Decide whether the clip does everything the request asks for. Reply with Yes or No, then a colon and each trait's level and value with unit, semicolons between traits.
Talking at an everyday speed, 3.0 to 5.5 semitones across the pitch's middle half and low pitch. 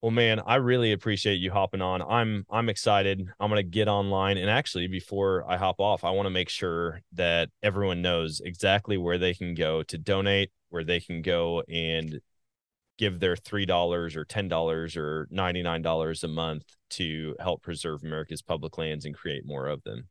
Yes: average, 195 wpm; average, 3.4 semitones; very low, 90 Hz